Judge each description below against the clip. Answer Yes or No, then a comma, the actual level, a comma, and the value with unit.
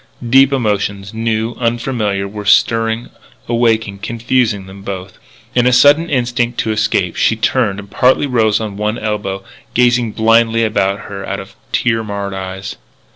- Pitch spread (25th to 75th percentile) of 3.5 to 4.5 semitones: No, average, 3.1 semitones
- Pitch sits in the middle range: No, low, 110 Hz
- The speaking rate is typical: Yes, average, 150 wpm